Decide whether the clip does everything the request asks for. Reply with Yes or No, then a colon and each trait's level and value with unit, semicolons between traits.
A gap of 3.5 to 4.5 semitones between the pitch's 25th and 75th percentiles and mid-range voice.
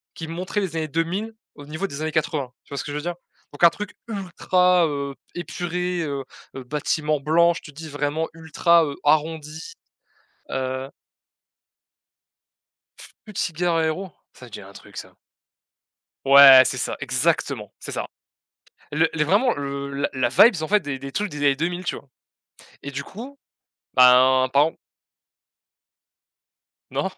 Yes: average, 3.8 semitones; medium, 155 Hz